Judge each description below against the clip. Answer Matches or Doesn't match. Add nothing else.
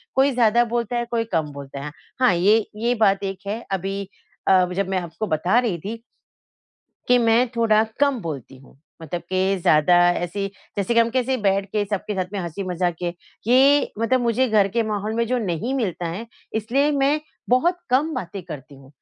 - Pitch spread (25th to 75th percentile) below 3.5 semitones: Doesn't match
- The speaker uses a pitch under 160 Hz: Doesn't match